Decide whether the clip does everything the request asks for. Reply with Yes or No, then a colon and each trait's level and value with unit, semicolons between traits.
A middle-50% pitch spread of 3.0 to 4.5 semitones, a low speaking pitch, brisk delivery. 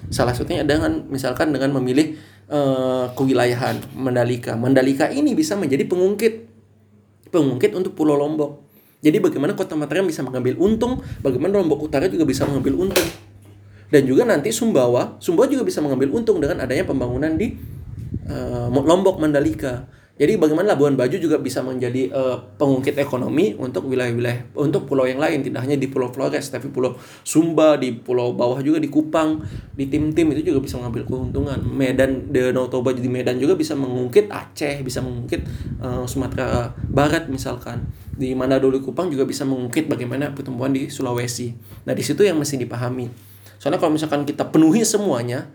Yes: average, 3.3 semitones; low, 130 Hz; fast, 160 wpm